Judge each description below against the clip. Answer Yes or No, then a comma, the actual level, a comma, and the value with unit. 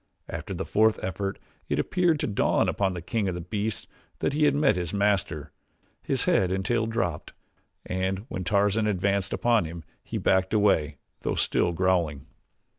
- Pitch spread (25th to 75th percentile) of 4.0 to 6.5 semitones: No, average, 3.2 semitones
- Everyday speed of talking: Yes, average, 170 wpm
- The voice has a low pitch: Yes, very low, 95 Hz